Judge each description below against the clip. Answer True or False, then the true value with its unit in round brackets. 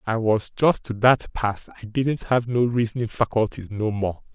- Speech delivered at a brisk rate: False (195 wpm)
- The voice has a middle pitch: False (115 Hz)